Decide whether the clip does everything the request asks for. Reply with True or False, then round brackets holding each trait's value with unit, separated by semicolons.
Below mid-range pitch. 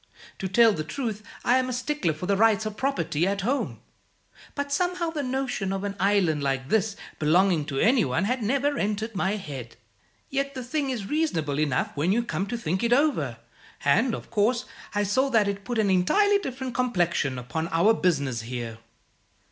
False (205 Hz)